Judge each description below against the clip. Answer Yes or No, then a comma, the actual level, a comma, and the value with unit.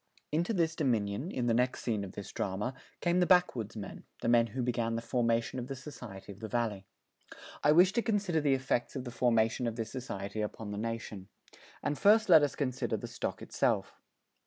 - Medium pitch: No, low, 120 Hz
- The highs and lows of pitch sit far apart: No, average, 5.0 semitones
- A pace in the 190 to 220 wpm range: Yes, average, 200 wpm